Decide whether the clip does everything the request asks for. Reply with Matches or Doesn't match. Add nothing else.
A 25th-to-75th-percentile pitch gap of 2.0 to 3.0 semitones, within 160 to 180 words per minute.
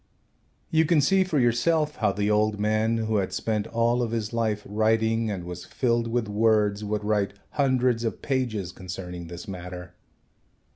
Matches